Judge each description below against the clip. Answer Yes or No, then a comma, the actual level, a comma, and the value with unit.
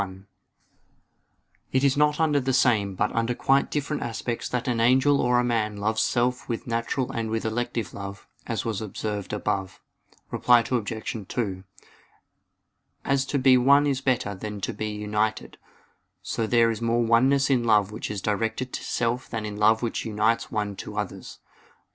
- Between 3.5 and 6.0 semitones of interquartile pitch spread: No, average, 3.0 semitones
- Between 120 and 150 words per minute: No, average, 170 wpm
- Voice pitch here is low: Yes, low, 115 Hz